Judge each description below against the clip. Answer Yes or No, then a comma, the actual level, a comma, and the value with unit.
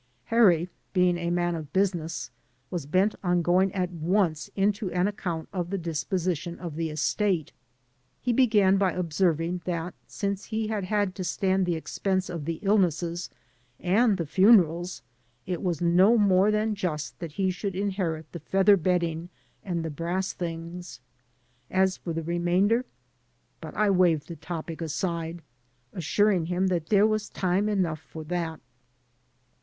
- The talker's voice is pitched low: No, medium, 180 Hz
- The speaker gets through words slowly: No, average, 155 wpm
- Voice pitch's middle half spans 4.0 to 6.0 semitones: No, average, 2.7 semitones